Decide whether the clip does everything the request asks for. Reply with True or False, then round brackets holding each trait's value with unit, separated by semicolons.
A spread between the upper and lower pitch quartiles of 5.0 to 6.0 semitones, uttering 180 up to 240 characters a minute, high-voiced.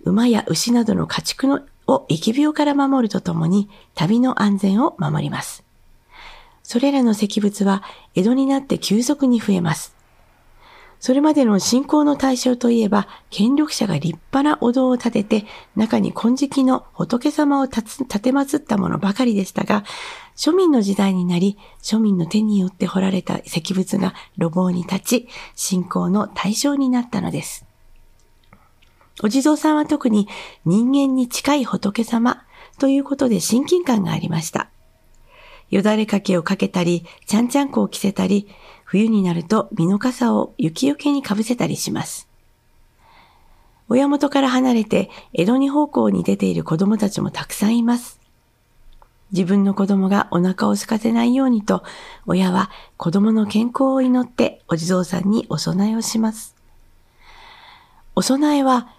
False (5.5 semitones; 295 characters per minute; 225 Hz)